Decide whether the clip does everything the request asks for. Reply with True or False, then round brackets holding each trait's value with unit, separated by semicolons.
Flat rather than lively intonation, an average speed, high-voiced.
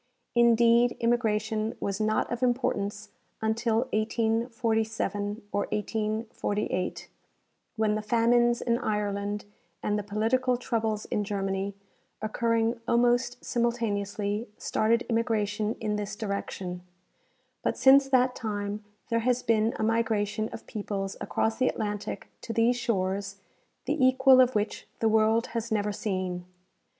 False (2.3 semitones; 125 wpm; 220 Hz)